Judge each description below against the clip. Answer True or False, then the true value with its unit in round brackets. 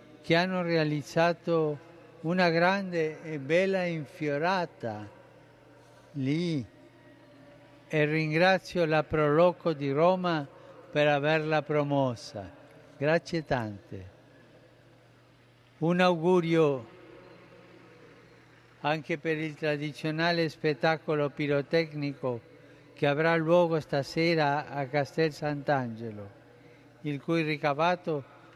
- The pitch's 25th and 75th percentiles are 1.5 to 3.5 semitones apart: True (2.5 semitones)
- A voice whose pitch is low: False (150 Hz)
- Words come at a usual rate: False (80 wpm)